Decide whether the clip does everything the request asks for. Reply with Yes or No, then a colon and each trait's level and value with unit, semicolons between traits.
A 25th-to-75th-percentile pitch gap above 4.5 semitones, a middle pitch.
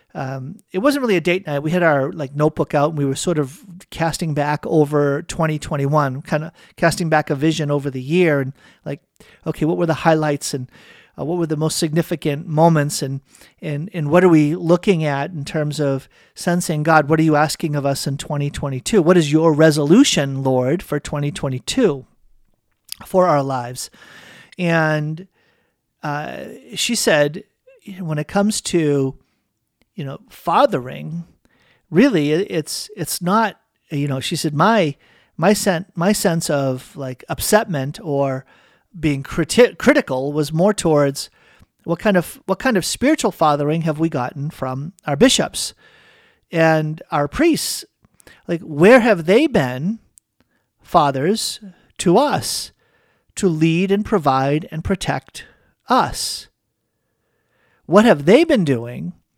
No: average, 4.0 semitones; medium, 160 Hz